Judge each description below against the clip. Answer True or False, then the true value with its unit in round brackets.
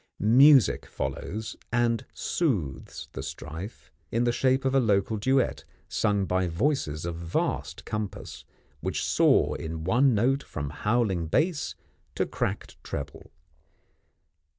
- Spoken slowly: True (125 wpm)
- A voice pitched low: True (110 Hz)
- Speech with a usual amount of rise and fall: False (7.3 semitones)